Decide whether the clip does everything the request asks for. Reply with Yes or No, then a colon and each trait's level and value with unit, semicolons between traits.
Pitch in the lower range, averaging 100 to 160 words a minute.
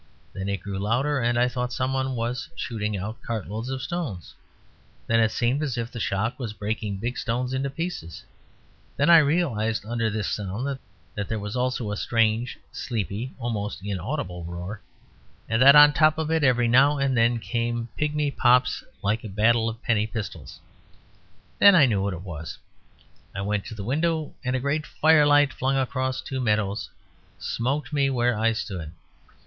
No: low, 120 Hz; average, 175 wpm